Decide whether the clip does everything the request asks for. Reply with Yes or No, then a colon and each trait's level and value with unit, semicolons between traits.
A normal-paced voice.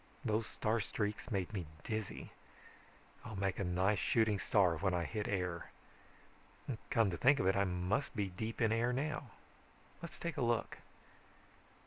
Yes: average, 160 wpm